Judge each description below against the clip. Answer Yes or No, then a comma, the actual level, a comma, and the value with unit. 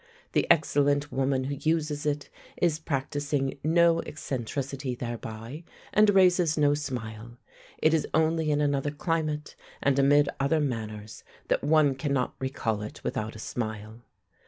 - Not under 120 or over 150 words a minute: Yes, slow, 135 wpm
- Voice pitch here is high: No, medium, 145 Hz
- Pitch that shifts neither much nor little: Yes, average, 3.5 semitones